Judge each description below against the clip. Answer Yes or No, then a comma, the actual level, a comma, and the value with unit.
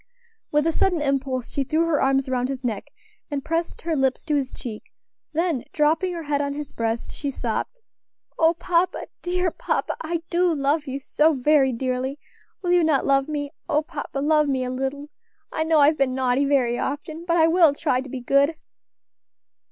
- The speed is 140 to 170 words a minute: No, average, 190 wpm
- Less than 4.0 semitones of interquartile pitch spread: Yes, average, 3.3 semitones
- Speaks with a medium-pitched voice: No, very high, 285 Hz